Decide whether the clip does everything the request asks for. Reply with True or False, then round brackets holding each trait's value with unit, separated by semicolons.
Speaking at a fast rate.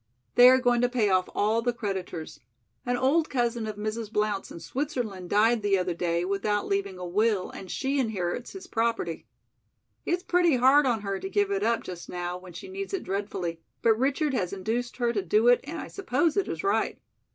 True (210 wpm)